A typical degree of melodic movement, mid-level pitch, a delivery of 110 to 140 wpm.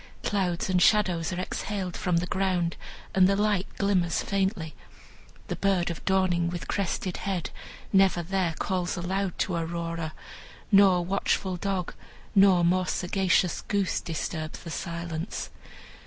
No: narrow, 2.2 semitones; medium, 180 Hz; slow, 135 wpm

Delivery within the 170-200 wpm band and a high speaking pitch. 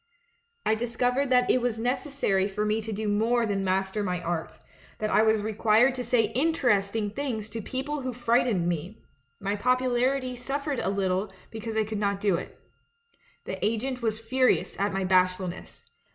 Yes: average, 180 wpm; high, 220 Hz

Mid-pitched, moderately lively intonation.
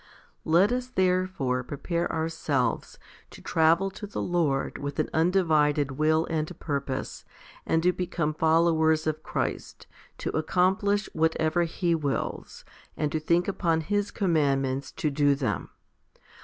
Yes: medium, 160 Hz; average, 3.2 semitones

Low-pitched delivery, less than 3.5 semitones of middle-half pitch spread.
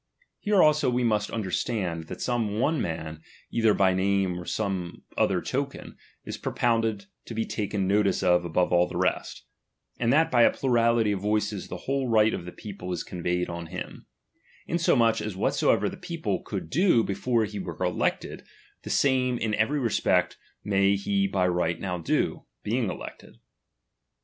No: low, 105 Hz; average, 4.4 semitones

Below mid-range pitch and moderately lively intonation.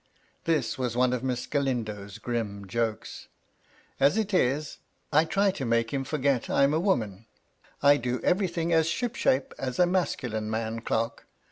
No: low, 130 Hz; wide, 5.7 semitones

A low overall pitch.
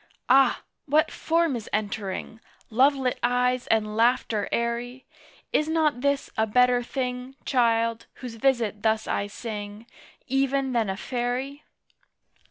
No: high, 245 Hz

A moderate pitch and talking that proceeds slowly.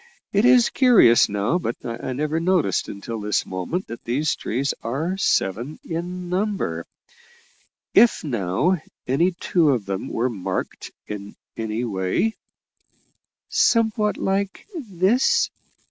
Yes: medium, 155 Hz; slow, 125 wpm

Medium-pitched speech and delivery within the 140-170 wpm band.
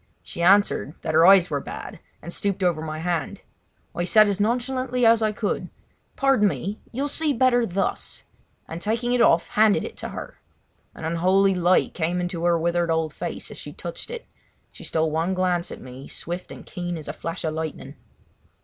No: medium, 180 Hz; average, 195 wpm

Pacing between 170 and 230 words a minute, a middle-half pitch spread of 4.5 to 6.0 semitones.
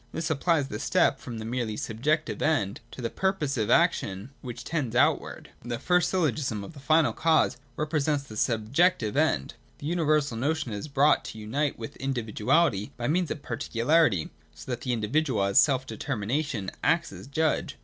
Yes: average, 180 wpm; wide, 5.6 semitones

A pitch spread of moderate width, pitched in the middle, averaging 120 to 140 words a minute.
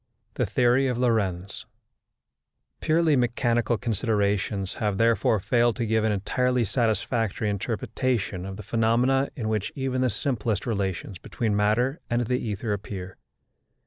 No: average, 3.2 semitones; low, 115 Hz; slow, 135 wpm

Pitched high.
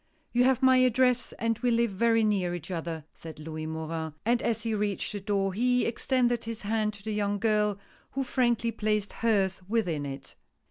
Yes: high, 215 Hz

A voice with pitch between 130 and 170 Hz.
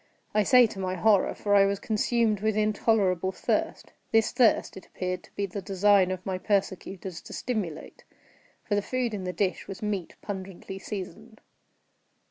No: high, 200 Hz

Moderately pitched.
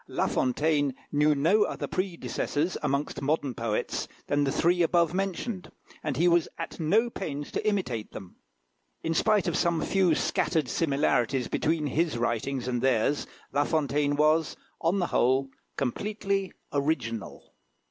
Yes: medium, 150 Hz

